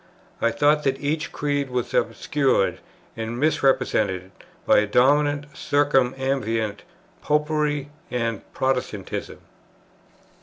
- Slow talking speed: Yes, slow, 90 wpm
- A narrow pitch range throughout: No, average, 4.0 semitones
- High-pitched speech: No, low, 135 Hz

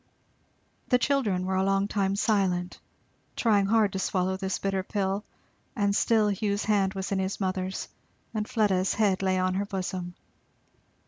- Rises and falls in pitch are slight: Yes, narrow, 1.7 semitones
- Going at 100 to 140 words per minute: No, average, 155 wpm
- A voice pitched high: Yes, high, 195 Hz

